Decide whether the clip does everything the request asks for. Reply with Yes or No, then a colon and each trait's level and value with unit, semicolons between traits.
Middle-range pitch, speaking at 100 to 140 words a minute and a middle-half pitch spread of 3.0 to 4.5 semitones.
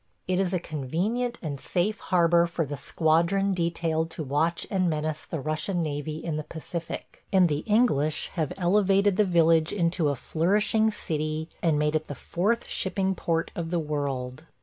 No: medium, 165 Hz; average, 170 wpm; average, 3.4 semitones